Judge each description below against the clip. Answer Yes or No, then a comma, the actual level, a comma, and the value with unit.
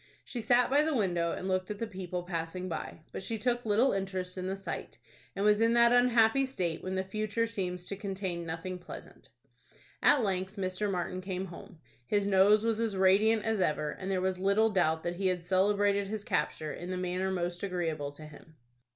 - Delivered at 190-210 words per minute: Yes, fast, 205 wpm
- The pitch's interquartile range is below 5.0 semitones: Yes, average, 2.9 semitones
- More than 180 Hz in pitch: Yes, high, 190 Hz